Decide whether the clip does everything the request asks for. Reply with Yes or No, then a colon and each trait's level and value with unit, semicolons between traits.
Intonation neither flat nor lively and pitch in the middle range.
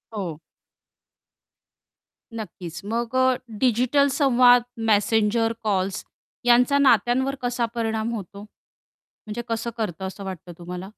No: average, 3.8 semitones; high, 225 Hz